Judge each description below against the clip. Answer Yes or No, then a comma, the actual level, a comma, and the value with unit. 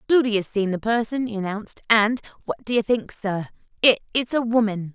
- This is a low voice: No, high, 220 Hz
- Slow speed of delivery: No, average, 195 wpm